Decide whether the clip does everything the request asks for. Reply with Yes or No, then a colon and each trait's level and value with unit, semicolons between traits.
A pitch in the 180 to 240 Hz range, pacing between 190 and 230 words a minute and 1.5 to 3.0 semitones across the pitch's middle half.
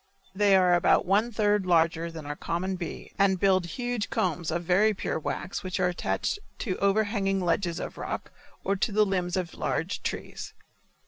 No: medium, 185 Hz; average, 180 wpm; narrow, 2.5 semitones